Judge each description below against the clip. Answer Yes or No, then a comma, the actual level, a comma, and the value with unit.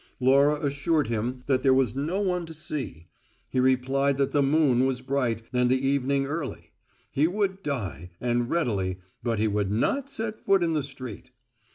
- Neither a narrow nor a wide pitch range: Yes, average, 3.6 semitones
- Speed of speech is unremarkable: Yes, average, 180 wpm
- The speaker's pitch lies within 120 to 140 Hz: Yes, low, 135 Hz